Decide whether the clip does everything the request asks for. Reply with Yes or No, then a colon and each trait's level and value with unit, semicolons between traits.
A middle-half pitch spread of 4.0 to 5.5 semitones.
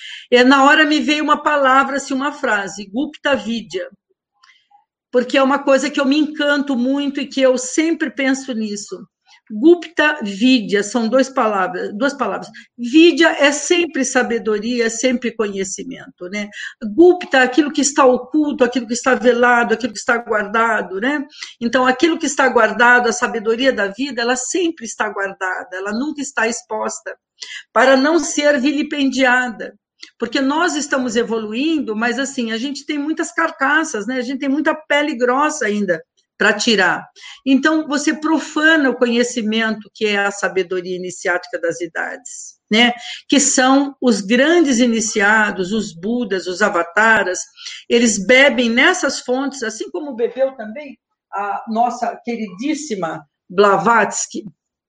Yes: average, 4.7 semitones